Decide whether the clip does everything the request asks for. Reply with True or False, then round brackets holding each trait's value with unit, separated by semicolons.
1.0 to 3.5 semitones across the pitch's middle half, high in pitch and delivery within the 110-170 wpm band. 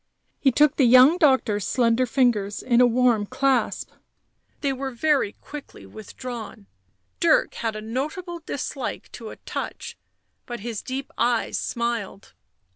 True (3.0 semitones; 250 Hz; 140 wpm)